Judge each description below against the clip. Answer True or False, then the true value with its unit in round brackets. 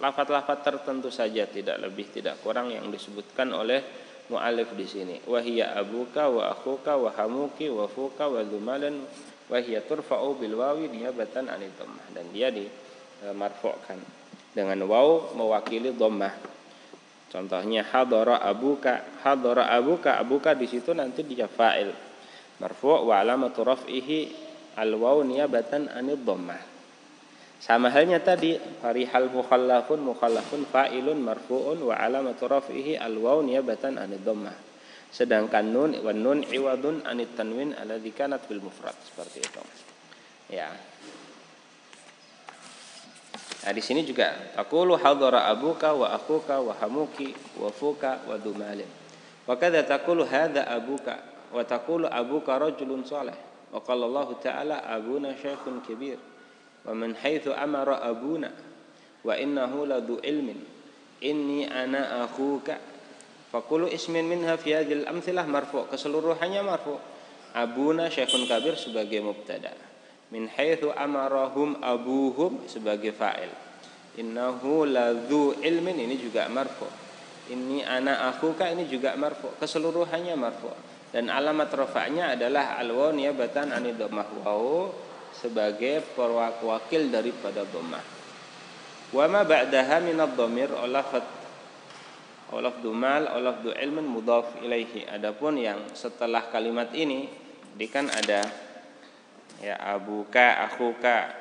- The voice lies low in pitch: True (130 Hz)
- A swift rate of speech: False (115 wpm)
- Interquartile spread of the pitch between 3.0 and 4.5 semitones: True (4.0 semitones)